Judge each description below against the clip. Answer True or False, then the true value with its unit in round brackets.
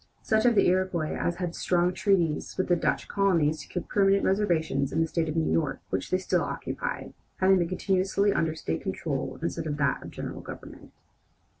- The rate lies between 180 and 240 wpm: True (195 wpm)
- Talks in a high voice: False (180 Hz)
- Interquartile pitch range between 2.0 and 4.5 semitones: True (3.3 semitones)